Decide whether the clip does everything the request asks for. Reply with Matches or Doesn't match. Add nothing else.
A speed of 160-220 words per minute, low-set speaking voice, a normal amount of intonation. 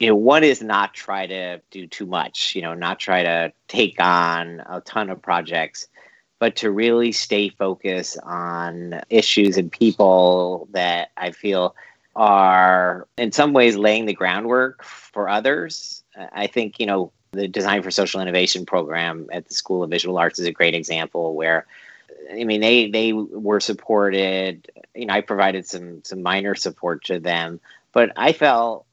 Matches